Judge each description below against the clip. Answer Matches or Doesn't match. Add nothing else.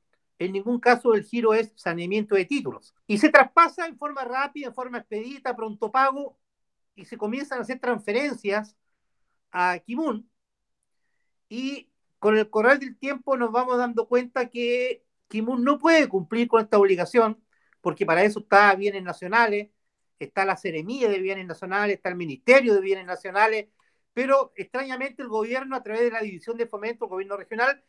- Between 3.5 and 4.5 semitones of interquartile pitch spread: Matches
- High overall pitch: Matches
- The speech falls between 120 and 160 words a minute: Doesn't match